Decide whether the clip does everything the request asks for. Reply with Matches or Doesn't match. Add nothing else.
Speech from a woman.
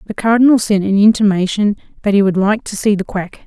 Matches